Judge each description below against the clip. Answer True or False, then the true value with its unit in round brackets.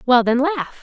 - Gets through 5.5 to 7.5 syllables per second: False (4.4 syllables/s)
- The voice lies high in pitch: True (265 Hz)